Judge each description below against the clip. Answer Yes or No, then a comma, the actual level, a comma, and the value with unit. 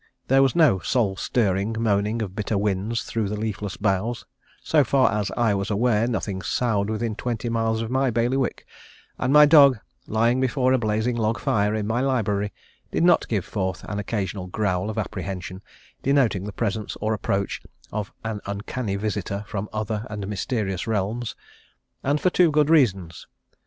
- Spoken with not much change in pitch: No, average, 3.2 semitones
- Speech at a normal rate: Yes, average, 170 wpm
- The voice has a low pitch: Yes, low, 110 Hz